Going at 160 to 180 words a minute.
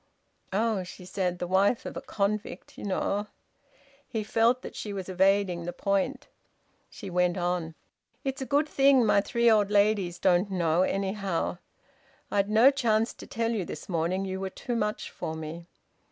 Yes: average, 170 wpm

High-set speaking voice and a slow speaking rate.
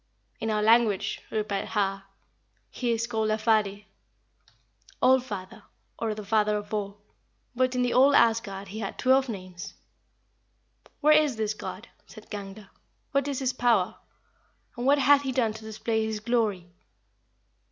No: high, 220 Hz; average, 150 wpm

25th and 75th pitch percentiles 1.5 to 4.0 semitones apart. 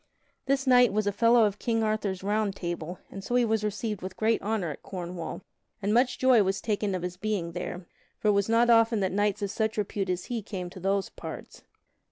Yes: average, 2.8 semitones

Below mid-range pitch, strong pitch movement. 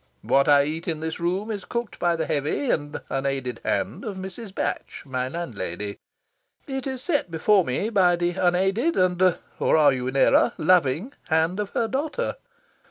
No: medium, 175 Hz; wide, 6.4 semitones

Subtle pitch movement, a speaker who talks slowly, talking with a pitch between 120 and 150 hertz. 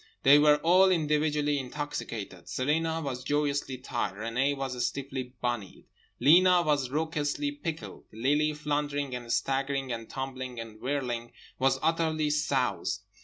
No: average, 3.0 semitones; slow, 125 wpm; medium, 140 Hz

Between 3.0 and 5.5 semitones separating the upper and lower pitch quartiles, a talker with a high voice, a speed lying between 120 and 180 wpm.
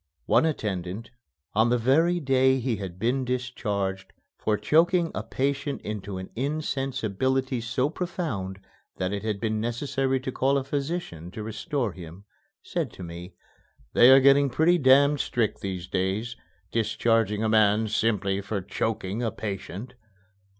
No: average, 5.1 semitones; low, 115 Hz; average, 145 wpm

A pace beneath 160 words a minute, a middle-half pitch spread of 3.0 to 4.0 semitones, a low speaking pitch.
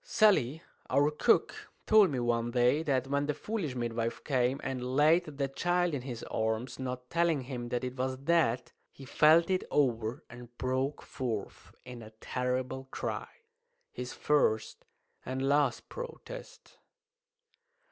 Yes: average, 145 wpm; average, 3.5 semitones; low, 130 Hz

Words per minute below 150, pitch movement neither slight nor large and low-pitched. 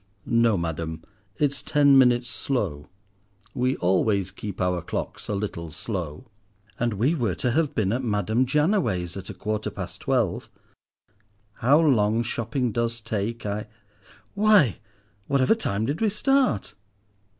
No: slow, 135 wpm; wide, 5.8 semitones; low, 115 Hz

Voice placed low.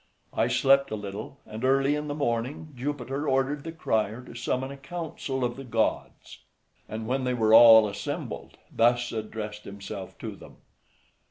Yes: low, 125 Hz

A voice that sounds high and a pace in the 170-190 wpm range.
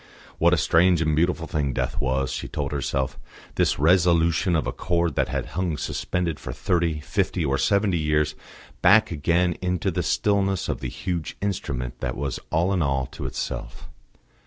No: very low, 80 Hz; average, 175 wpm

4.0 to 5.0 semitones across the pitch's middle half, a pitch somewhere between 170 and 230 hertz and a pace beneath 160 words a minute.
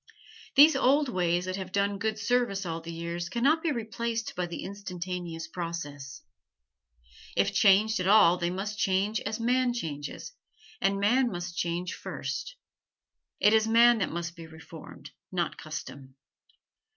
Yes: average, 4.6 semitones; high, 190 Hz; average, 150 wpm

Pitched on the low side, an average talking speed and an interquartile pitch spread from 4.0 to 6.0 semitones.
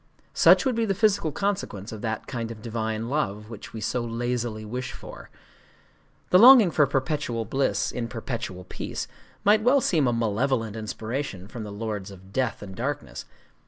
Yes: low, 115 Hz; average, 170 wpm; average, 5.1 semitones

